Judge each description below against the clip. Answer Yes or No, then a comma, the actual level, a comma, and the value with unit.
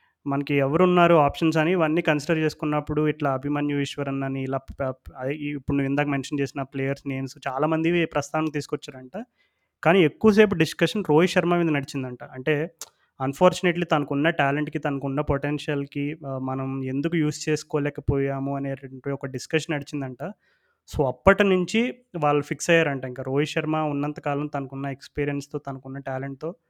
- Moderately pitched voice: Yes, medium, 145 Hz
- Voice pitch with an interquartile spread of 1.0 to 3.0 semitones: Yes, narrow, 2.6 semitones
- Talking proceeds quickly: Yes, fast, 130 wpm